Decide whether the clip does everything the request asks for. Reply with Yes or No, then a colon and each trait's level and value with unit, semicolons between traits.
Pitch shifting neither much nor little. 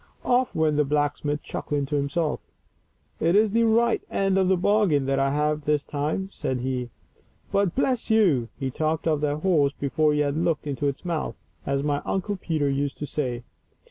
Yes: average, 4.6 semitones